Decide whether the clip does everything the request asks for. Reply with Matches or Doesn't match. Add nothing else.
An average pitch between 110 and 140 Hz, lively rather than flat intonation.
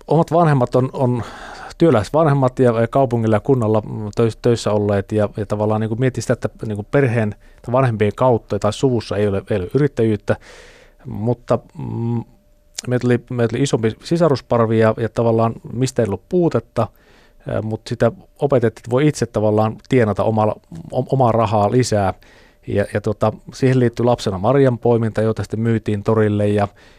Doesn't match